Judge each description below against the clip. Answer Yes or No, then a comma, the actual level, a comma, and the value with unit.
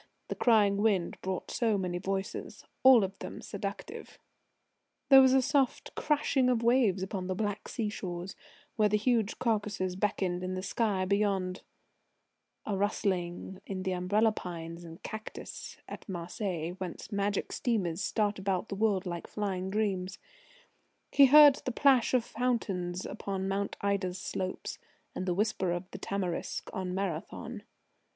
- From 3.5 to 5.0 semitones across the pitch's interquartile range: No, average, 3.1 semitones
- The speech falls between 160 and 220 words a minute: No, average, 150 wpm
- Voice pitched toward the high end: Yes, high, 200 Hz